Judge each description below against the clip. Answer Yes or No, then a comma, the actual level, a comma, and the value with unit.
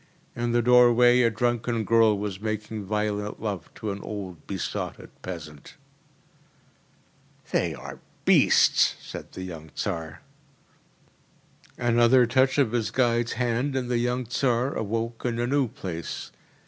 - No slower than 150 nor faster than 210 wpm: No, slow, 135 wpm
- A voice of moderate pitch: No, low, 115 Hz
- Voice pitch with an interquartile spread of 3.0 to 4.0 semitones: Yes, average, 3.4 semitones